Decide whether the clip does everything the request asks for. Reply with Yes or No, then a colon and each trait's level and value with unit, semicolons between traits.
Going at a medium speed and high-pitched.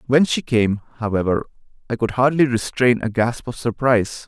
No: average, 170 wpm; low, 120 Hz